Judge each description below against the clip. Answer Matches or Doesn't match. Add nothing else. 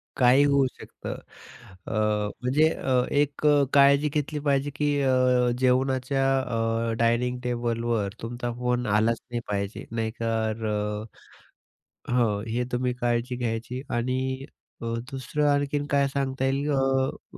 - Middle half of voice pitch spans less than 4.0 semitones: Matches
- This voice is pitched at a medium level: Doesn't match